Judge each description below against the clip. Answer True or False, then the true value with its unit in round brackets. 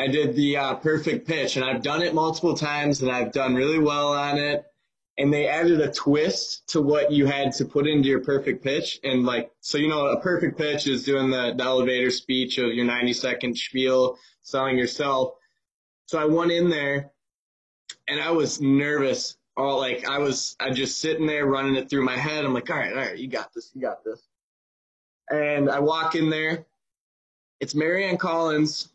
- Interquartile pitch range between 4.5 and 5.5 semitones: False (3.1 semitones)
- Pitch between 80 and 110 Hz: False (140 Hz)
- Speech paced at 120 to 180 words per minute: False (205 wpm)